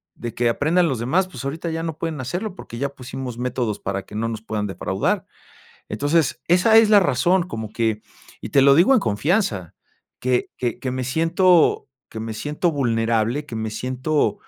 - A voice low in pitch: Yes, low, 130 Hz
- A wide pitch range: Yes, wide, 6.4 semitones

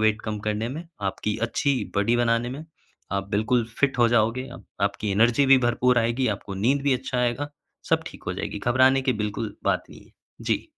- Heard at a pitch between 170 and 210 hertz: No, low, 120 Hz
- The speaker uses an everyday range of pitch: Yes, average, 3.3 semitones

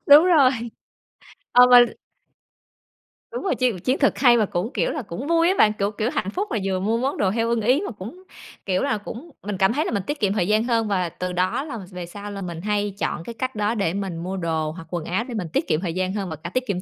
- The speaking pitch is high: Yes, high, 210 Hz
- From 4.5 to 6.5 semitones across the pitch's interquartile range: Yes, average, 5.1 semitones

